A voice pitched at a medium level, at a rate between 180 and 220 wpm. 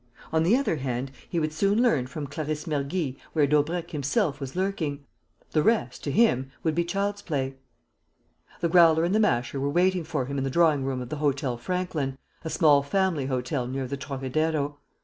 Yes: medium, 150 Hz; average, 190 wpm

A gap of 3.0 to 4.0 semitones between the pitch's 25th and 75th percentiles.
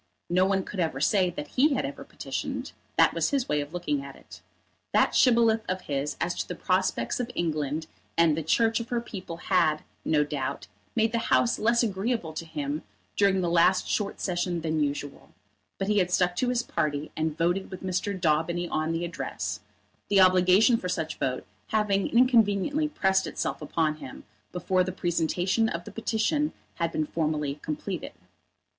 No: average, 4.8 semitones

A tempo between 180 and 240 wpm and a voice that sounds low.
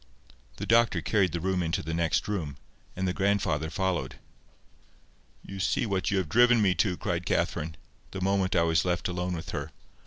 Yes: average, 185 wpm; very low, 90 Hz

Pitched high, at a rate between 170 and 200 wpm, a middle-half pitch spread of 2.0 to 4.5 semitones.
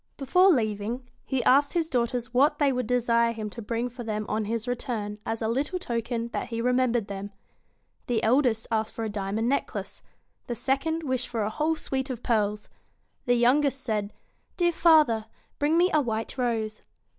Yes: high, 240 Hz; average, 180 wpm; average, 3.4 semitones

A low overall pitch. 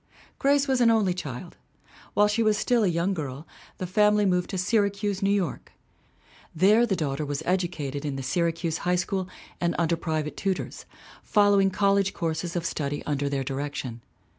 No: medium, 180 Hz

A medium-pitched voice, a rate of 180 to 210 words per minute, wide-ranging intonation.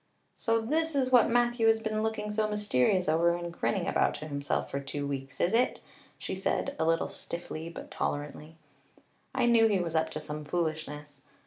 Yes: medium, 175 Hz; average, 190 wpm; wide, 6.5 semitones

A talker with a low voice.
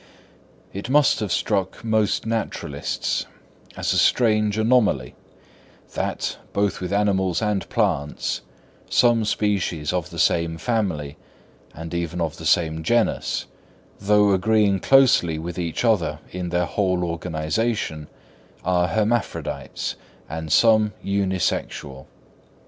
Yes: very low, 95 Hz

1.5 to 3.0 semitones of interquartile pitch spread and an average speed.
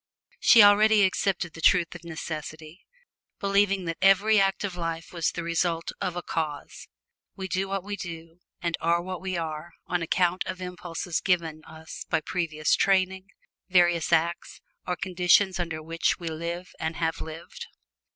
Yes: narrow, 2.4 semitones; average, 160 wpm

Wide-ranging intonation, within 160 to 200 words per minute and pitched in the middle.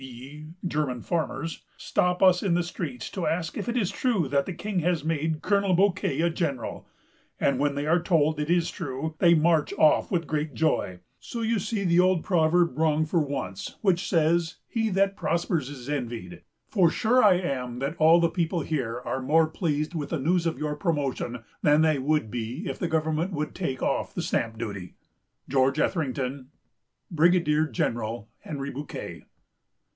No: average, 4.0 semitones; average, 180 wpm; medium, 155 Hz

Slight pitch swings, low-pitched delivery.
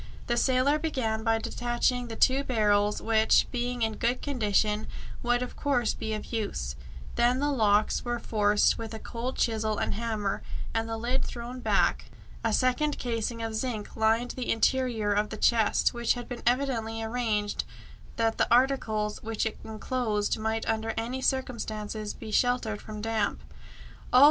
No: narrow, 2.3 semitones; high, 225 Hz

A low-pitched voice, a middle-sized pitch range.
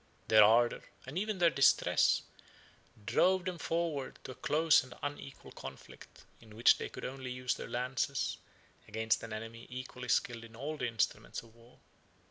Yes: low, 125 Hz; average, 4.1 semitones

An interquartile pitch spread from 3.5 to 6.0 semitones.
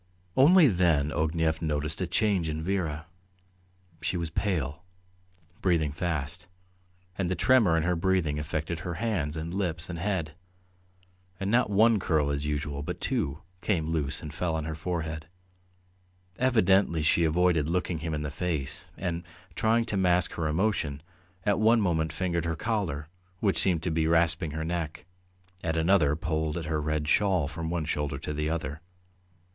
No: average, 3.1 semitones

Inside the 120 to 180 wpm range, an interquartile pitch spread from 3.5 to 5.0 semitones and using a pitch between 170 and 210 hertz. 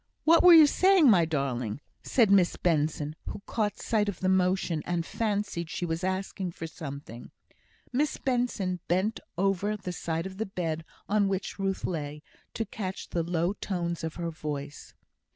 Yes: average, 170 wpm; average, 4.1 semitones; medium, 185 Hz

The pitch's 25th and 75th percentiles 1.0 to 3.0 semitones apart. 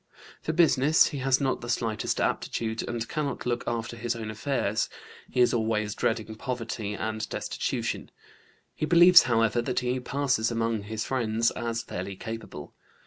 Yes: average, 2.7 semitones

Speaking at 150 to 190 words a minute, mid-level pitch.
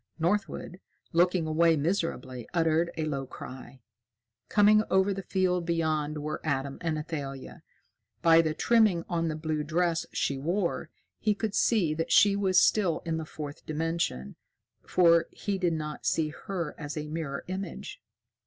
Yes: average, 155 wpm; medium, 165 Hz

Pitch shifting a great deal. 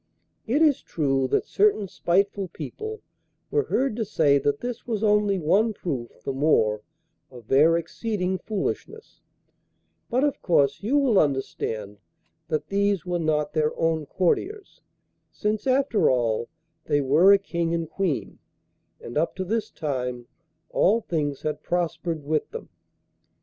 Yes: wide, 6.6 semitones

